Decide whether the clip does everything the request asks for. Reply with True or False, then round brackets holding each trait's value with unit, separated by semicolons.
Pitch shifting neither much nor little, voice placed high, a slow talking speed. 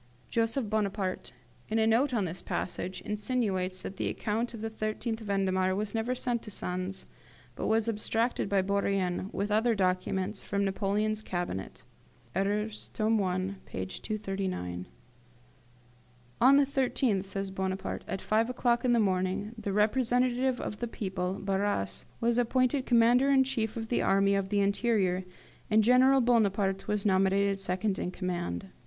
False (3.2 semitones; 205 Hz; 150 wpm)